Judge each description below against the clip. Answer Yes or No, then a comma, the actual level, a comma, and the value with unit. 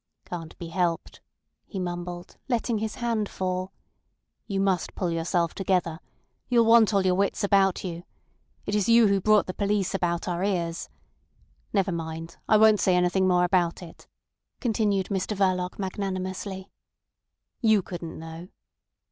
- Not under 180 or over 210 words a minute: No, average, 150 wpm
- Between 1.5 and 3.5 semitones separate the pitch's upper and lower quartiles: Yes, narrow, 2.5 semitones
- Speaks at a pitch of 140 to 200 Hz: Yes, medium, 185 Hz